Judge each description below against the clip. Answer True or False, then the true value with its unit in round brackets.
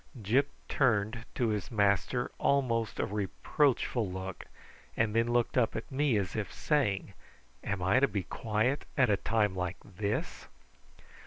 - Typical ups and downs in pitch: True (3.5 semitones)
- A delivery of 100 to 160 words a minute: True (150 wpm)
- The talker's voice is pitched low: True (110 Hz)